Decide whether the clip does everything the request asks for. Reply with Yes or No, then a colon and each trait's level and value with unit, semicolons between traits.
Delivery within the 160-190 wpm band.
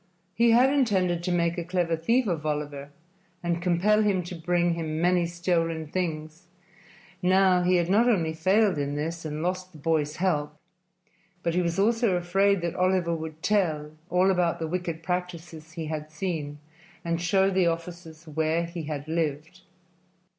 Yes: average, 170 wpm